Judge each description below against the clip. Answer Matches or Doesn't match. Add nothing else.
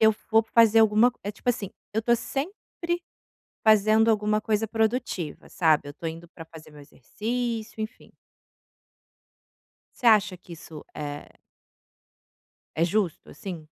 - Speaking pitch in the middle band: Doesn't match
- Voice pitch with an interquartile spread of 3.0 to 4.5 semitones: Doesn't match